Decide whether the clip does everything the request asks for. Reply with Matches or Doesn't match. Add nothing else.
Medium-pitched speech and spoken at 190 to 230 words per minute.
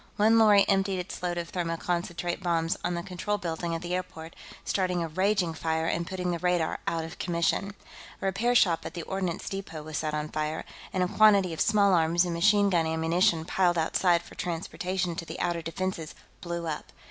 Matches